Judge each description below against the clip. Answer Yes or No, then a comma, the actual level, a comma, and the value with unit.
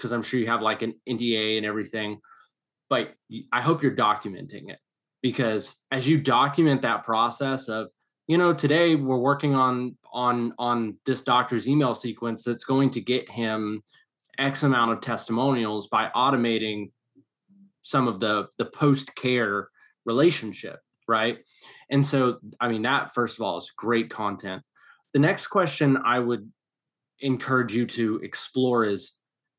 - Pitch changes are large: No, average, 3.2 semitones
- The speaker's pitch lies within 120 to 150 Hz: Yes, low, 125 Hz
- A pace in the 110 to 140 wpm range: No, average, 150 wpm